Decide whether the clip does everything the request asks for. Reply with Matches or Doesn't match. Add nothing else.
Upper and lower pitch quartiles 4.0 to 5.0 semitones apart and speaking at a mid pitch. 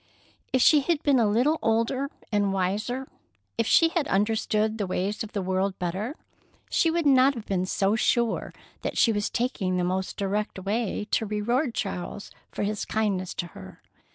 Doesn't match